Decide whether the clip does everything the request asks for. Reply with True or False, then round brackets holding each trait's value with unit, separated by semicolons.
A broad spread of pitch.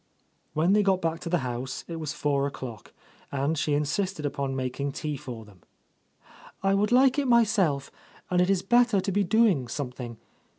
True (6.3 semitones)